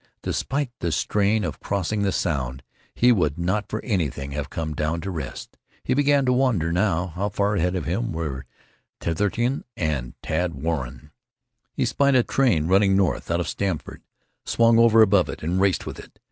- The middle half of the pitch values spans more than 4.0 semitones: Yes, wide, 5.4 semitones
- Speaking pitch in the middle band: No, very low, 95 Hz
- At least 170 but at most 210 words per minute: Yes, average, 175 wpm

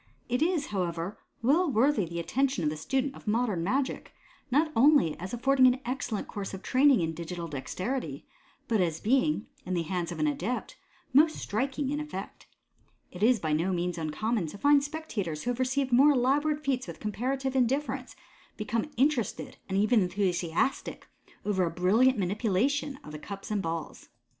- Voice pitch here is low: No, high, 230 Hz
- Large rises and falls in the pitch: Yes, wide, 6.9 semitones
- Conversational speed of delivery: Yes, average, 170 wpm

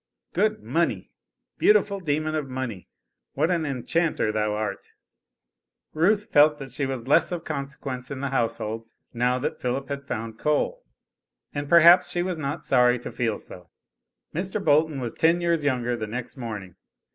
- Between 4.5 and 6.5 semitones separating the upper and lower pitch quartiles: Yes, average, 4.9 semitones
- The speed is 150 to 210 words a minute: Yes, average, 160 wpm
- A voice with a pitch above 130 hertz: Yes, medium, 140 Hz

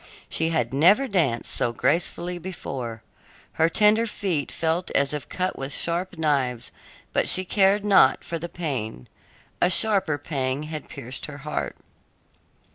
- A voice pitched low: No, medium, 160 Hz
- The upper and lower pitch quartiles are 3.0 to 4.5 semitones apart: No, average, 5.2 semitones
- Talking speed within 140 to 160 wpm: Yes, average, 145 wpm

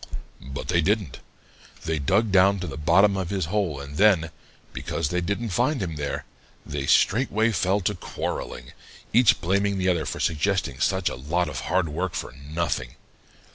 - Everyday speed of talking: Yes, average, 175 wpm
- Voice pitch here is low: Yes, very low, 90 Hz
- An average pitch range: Yes, average, 4.6 semitones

